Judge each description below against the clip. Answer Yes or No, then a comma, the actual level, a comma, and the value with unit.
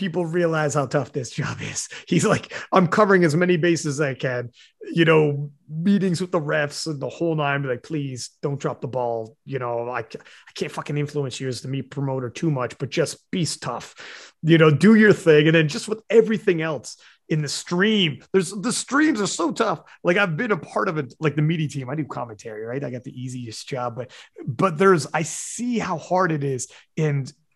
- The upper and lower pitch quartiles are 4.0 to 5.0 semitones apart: Yes, average, 4.7 semitones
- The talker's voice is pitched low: No, medium, 155 Hz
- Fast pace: Yes, fast, 220 wpm